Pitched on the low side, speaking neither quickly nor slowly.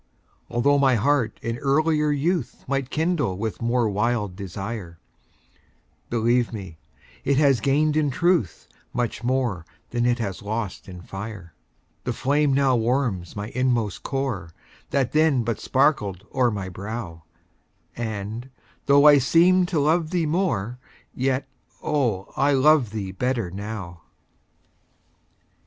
No: low, 120 Hz; slow, 130 wpm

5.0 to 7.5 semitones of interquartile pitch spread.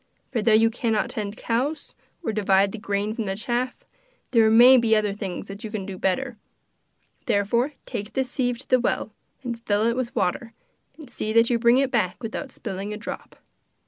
No: average, 2.9 semitones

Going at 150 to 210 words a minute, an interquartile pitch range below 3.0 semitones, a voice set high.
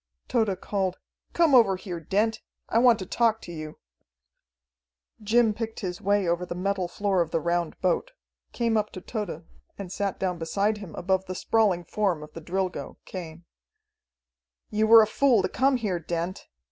No: average, 175 wpm; average, 3.8 semitones; high, 195 Hz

